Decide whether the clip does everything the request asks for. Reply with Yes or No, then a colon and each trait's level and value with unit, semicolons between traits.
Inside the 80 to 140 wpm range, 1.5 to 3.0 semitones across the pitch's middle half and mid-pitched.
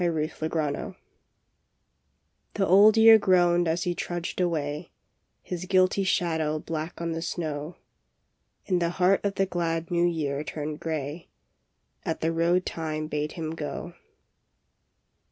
Yes: slow, 135 wpm; narrow, 2.4 semitones; medium, 165 Hz